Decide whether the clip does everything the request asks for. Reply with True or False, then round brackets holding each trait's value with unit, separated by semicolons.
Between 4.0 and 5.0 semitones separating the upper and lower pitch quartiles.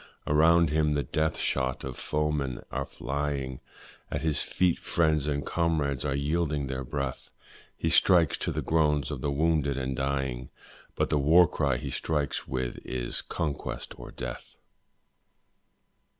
False (2.6 semitones)